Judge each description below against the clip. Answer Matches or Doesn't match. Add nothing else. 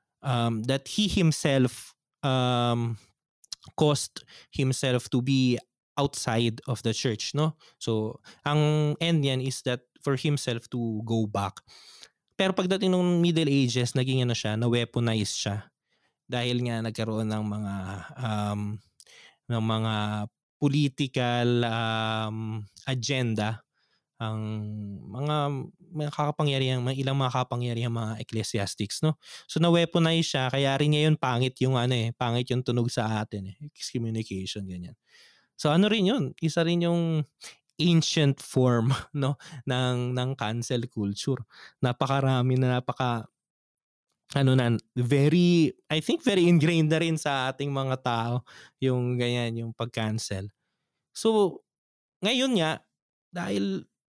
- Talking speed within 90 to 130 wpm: Matches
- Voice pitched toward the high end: Doesn't match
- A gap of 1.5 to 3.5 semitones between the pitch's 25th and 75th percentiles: Doesn't match